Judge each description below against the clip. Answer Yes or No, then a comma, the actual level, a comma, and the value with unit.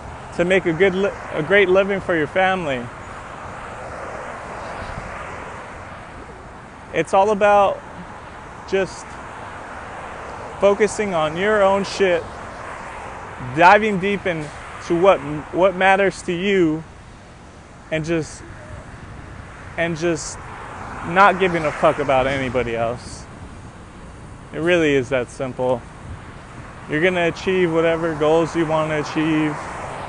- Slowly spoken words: Yes, slow, 110 wpm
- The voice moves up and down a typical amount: No, wide, 5.8 semitones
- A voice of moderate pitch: Yes, medium, 165 Hz